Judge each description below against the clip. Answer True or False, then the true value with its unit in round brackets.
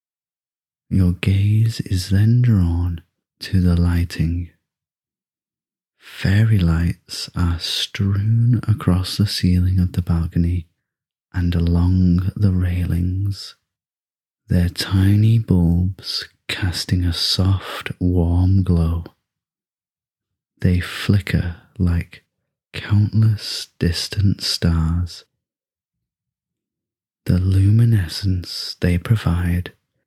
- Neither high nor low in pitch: False (90 Hz)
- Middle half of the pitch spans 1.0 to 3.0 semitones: True (2.4 semitones)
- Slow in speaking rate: True (80 wpm)